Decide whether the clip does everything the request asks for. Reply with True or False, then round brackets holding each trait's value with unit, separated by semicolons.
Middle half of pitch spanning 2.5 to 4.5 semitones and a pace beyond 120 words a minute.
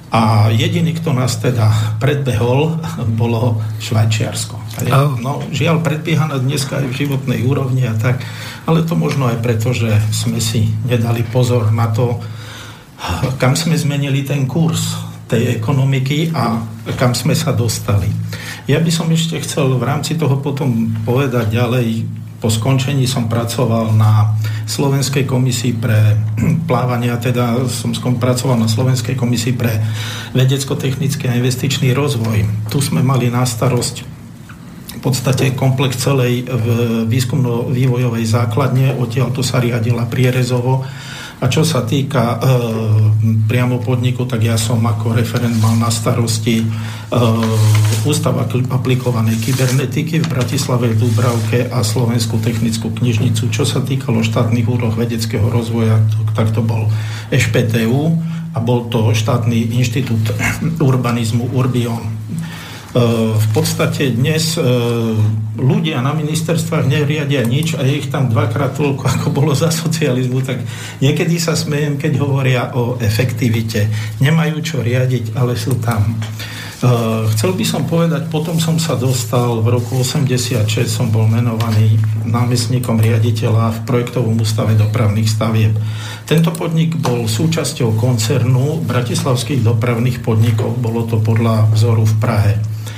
True (3.0 semitones; 130 wpm)